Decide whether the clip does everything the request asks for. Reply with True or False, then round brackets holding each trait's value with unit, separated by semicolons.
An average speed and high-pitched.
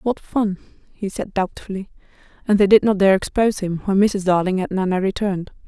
True (190 wpm; 195 Hz)